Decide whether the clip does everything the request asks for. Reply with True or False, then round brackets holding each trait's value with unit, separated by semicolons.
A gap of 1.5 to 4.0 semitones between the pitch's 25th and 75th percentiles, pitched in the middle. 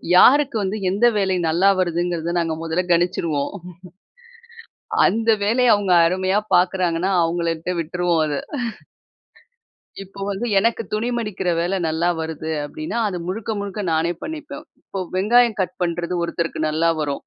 True (3.5 semitones; 180 Hz)